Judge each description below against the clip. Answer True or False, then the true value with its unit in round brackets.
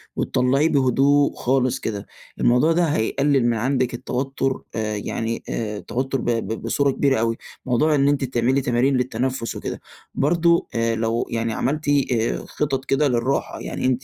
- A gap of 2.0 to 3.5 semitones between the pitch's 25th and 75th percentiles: True (3.0 semitones)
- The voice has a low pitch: True (130 Hz)